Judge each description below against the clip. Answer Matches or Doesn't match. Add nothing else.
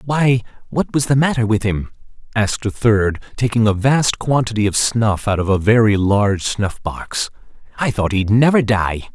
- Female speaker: Doesn't match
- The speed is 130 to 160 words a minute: Doesn't match